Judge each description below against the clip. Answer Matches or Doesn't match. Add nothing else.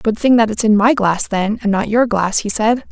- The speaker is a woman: Matches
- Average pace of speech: Doesn't match